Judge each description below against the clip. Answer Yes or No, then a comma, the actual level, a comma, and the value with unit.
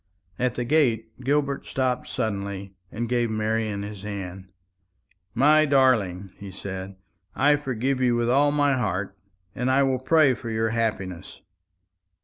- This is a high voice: No, low, 115 Hz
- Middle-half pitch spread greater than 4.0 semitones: Yes, average, 4.8 semitones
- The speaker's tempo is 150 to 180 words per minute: No, average, 140 wpm